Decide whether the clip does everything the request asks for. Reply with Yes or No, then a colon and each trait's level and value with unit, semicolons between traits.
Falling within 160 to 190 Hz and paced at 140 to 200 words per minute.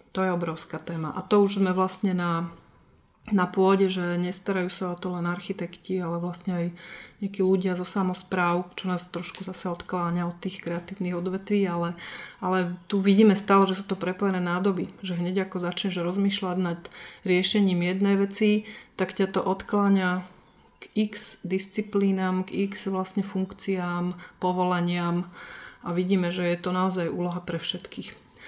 Yes: medium, 185 Hz; average, 160 wpm